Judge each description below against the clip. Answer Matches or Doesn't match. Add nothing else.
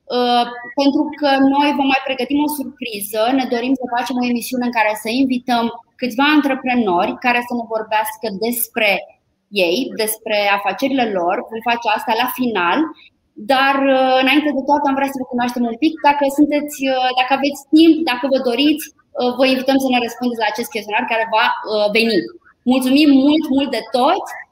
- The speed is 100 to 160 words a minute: Doesn't match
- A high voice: Matches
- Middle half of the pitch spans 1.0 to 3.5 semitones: Matches